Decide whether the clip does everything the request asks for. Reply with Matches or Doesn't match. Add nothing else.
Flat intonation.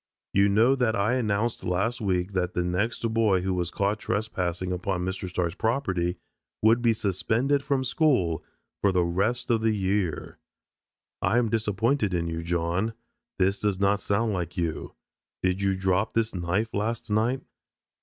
Doesn't match